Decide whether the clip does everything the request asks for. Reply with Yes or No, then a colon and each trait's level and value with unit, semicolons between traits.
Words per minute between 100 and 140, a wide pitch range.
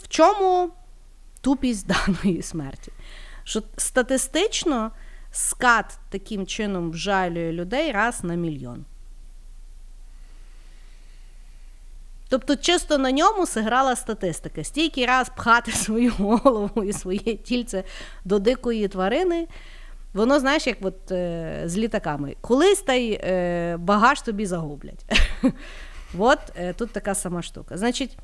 Yes: average, 110 wpm; wide, 6.3 semitones